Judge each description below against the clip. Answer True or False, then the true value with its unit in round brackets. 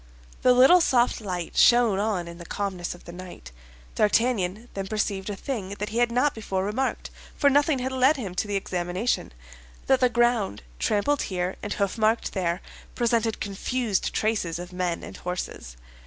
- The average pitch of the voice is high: True (205 Hz)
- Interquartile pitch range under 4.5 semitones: False (4.9 semitones)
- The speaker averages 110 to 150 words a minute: False (165 wpm)